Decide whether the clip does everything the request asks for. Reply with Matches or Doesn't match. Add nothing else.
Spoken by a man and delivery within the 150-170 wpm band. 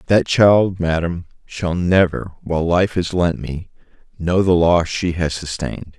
Matches